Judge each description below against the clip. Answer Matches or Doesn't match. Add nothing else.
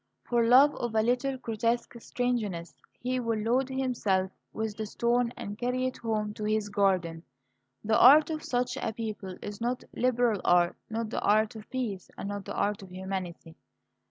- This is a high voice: Matches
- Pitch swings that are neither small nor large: Matches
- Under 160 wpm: Doesn't match